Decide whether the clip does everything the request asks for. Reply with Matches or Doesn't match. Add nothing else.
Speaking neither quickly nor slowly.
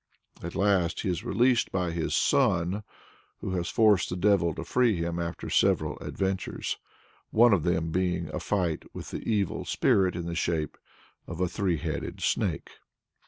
Matches